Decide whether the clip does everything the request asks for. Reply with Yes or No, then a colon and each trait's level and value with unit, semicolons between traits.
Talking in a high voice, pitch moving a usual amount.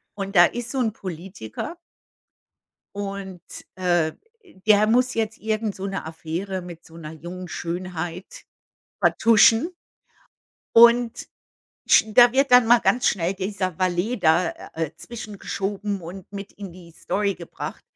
Yes: high, 195 Hz; average, 4.1 semitones